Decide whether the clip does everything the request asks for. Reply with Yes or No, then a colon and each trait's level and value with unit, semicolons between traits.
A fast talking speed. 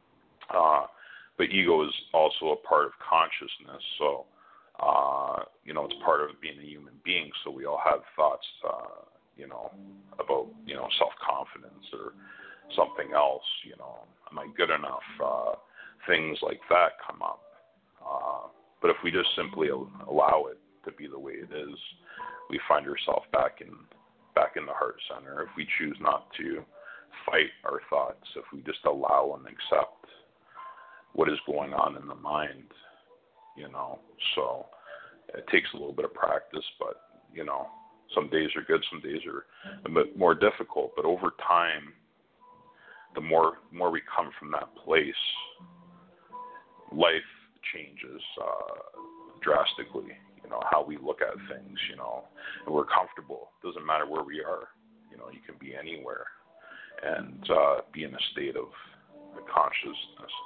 No: average, 165 wpm